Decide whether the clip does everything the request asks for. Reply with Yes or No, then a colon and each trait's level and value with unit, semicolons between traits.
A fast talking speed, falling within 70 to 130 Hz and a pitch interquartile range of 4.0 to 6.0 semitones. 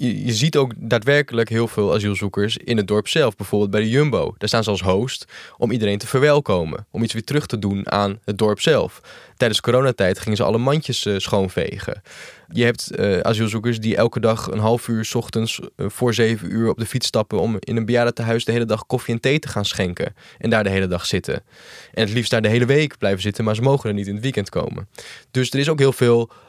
No: fast, 230 wpm; low, 115 Hz; average, 2.9 semitones